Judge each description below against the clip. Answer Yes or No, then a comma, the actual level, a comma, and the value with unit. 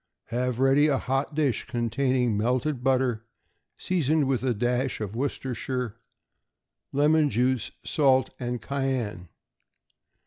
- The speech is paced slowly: Yes, slow, 110 wpm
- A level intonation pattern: Yes, narrow, 2.3 semitones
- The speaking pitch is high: No, low, 130 Hz